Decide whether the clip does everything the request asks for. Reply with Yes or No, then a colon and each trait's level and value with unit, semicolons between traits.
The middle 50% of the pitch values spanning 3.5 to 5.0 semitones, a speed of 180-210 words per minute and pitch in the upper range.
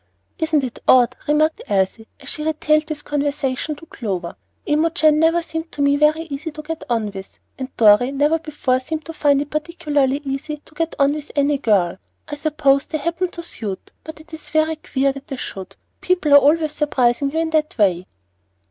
No: average, 3.0 semitones; average, 200 wpm; very high, 295 Hz